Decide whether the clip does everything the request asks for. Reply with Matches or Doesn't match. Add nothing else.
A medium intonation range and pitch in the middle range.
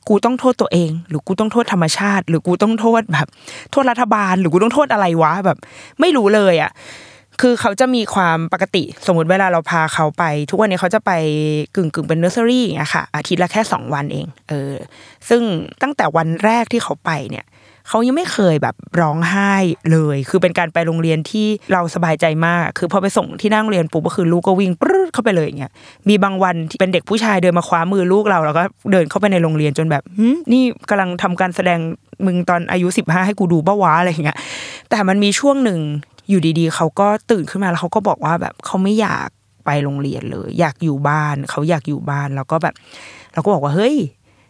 Matches